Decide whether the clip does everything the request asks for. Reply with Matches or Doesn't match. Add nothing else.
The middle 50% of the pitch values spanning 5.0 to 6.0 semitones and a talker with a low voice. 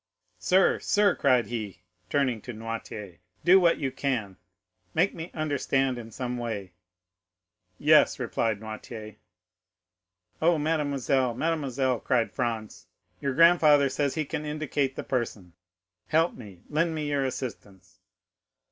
Matches